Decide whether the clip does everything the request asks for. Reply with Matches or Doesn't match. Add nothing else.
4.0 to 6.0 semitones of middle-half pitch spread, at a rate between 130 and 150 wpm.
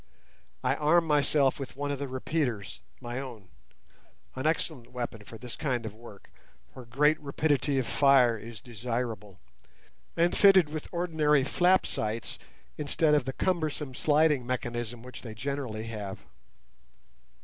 Matches